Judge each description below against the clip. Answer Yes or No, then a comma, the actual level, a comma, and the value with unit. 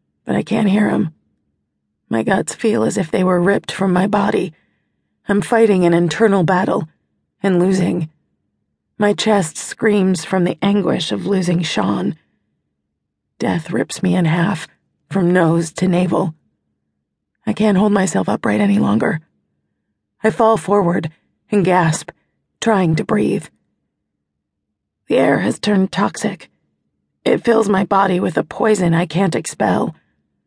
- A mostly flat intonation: No, average, 4.1 semitones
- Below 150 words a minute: Yes, average, 140 wpm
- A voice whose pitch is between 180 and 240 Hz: Yes, medium, 185 Hz